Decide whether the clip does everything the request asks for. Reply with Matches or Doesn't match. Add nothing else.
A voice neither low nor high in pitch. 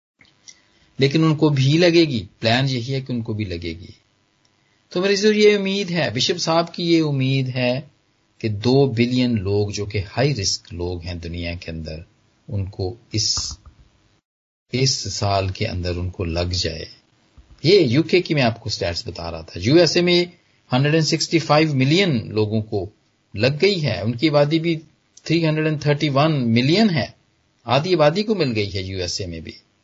Doesn't match